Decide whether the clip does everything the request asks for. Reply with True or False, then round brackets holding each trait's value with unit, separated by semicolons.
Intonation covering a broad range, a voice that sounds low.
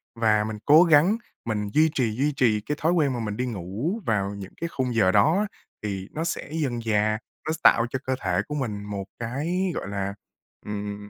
True (6.3 semitones; 115 Hz)